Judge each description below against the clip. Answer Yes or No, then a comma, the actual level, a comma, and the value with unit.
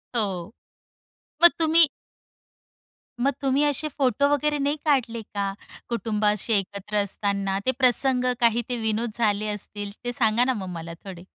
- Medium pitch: No, high, 230 Hz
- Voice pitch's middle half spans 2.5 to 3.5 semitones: No, average, 4.7 semitones